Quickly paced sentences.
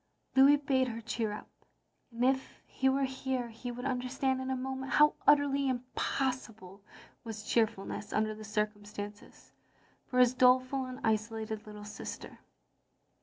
No: average, 150 wpm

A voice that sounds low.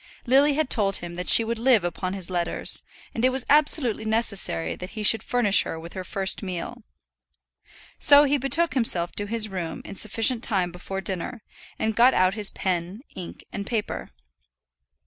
No: high, 210 Hz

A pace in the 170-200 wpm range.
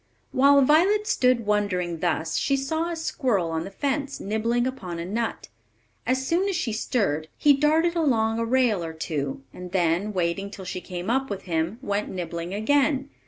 Yes: average, 180 wpm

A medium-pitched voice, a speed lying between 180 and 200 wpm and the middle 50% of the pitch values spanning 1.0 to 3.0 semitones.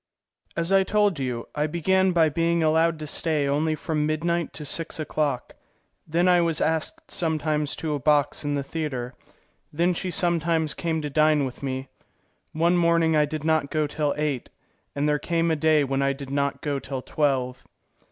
Yes: medium, 155 Hz; average, 185 wpm; narrow, 2.6 semitones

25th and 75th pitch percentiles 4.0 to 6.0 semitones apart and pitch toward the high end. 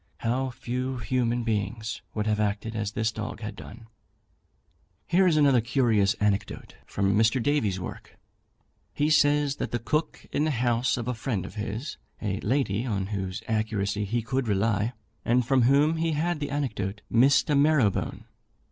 No: average, 4.4 semitones; low, 115 Hz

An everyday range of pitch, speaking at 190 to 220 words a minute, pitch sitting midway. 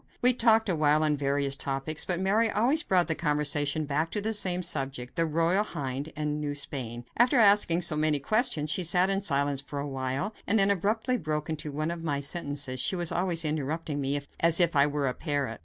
Yes: average, 4.5 semitones; fast, 205 wpm; medium, 155 Hz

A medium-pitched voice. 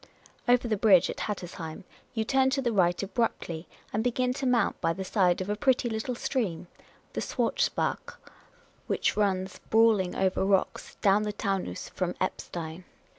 No: high, 205 Hz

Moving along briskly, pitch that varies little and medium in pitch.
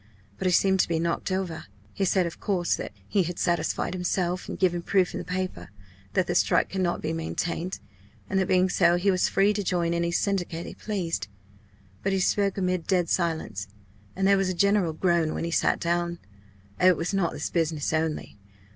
Yes: fast, 210 wpm; narrow, 2.1 semitones; medium, 180 Hz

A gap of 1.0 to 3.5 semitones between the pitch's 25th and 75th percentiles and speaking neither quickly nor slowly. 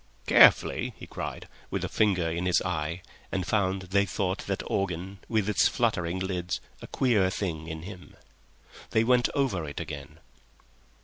Yes: average, 2.7 semitones; average, 160 wpm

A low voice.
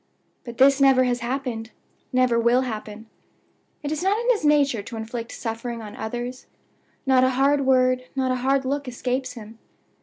No: very high, 255 Hz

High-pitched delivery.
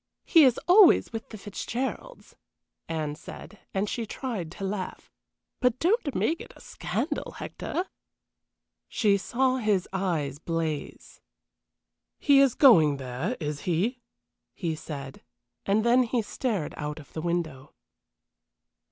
Yes: high, 200 Hz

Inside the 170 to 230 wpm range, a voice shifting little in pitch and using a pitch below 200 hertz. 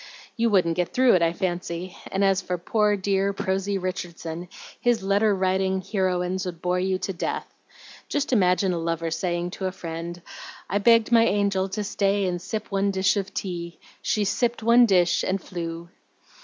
Yes: average, 180 wpm; narrow, 2.3 semitones; high, 190 Hz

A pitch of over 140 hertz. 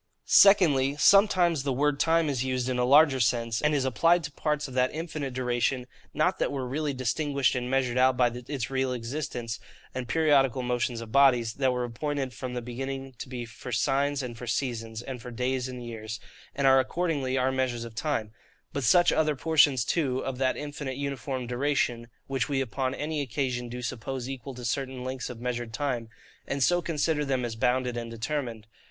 No: low, 130 Hz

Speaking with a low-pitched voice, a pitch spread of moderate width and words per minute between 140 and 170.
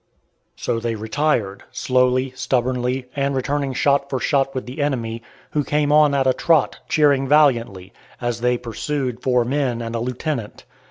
Yes: low, 130 Hz; average, 3.0 semitones; average, 160 wpm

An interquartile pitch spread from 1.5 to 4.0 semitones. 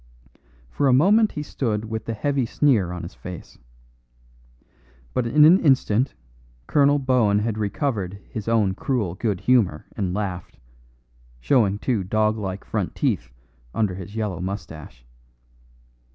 No: average, 5.2 semitones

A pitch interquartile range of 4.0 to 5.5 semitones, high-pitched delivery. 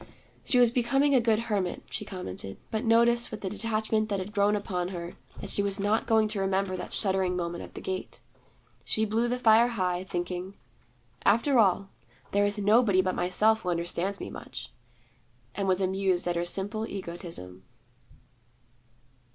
No: average, 3.2 semitones; high, 200 Hz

